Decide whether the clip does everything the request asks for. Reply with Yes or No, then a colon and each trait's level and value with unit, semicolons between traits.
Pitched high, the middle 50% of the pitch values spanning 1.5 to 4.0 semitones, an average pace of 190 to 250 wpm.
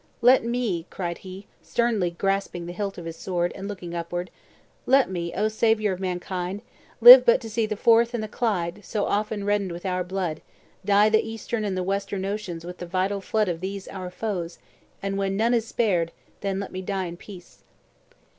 Yes: high, 195 Hz; average, 3.2 semitones; average, 200 wpm